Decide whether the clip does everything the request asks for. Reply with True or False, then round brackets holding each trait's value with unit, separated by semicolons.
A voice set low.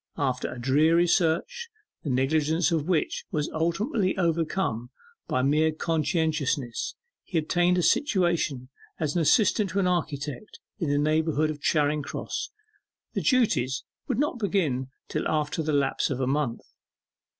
False (155 Hz)